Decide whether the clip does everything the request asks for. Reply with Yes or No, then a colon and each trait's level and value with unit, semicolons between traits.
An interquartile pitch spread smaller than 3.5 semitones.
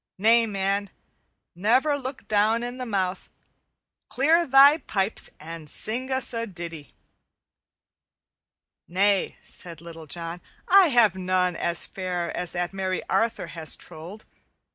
No: wide, 5.4 semitones